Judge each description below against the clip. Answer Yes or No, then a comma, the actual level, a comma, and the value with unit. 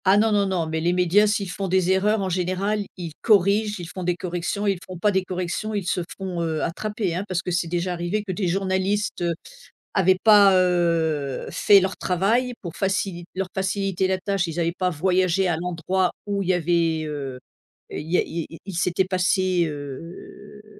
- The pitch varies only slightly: Yes, narrow, 2.3 semitones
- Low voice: No, medium, 185 Hz